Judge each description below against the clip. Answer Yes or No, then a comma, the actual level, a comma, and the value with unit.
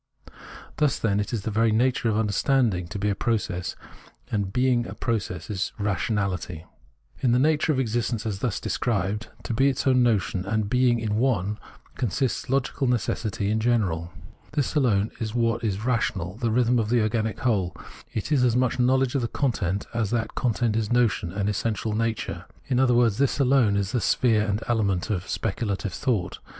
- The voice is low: Yes, low, 115 Hz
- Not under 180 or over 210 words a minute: Yes, average, 190 wpm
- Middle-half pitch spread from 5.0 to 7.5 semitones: No, average, 3.4 semitones